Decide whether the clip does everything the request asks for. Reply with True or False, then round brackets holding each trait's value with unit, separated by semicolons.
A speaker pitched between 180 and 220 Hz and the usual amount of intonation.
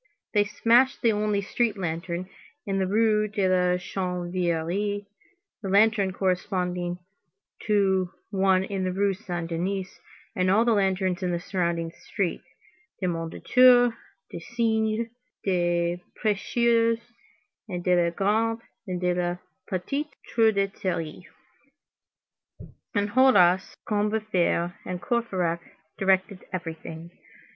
True (190 Hz; 3.1 semitones)